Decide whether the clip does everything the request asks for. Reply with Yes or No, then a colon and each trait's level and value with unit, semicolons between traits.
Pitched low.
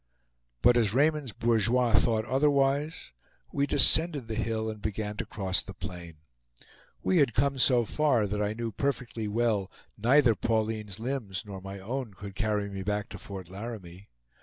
Yes: low, 110 Hz